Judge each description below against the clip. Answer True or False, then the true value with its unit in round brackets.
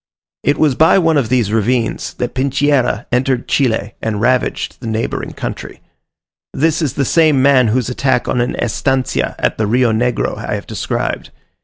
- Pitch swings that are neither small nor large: True (3.2 semitones)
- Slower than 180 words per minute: True (170 wpm)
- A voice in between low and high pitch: False (125 Hz)